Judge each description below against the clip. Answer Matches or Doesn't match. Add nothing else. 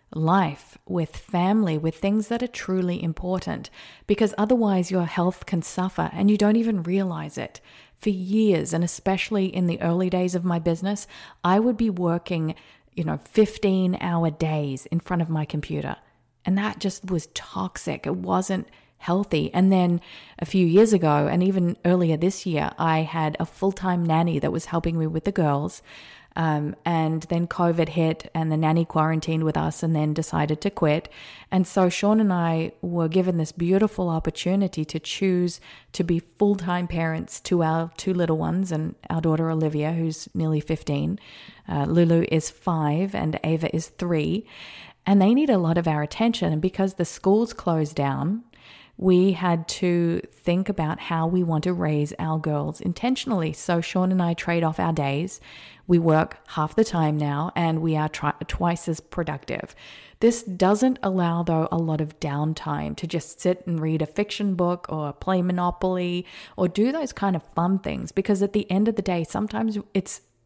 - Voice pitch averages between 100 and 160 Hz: Doesn't match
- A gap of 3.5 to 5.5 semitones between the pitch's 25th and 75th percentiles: Doesn't match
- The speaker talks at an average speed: Matches